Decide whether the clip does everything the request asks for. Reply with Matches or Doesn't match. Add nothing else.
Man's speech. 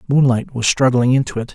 Matches